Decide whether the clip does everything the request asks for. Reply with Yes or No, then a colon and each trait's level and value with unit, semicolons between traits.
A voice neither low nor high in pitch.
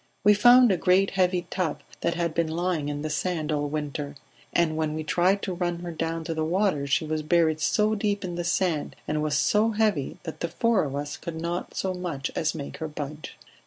Yes: medium, 170 Hz